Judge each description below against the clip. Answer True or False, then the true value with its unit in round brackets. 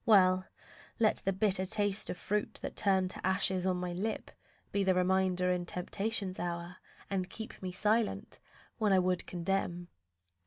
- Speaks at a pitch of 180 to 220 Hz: True (190 Hz)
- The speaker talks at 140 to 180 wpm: True (160 wpm)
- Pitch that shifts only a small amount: True (1.8 semitones)